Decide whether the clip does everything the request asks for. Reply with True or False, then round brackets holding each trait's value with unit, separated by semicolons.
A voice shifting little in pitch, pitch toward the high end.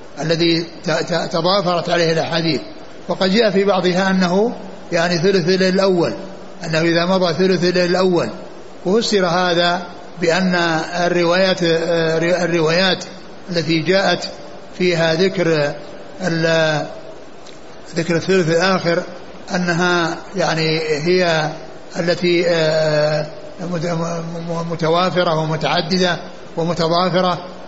False (1.7 semitones; 175 Hz)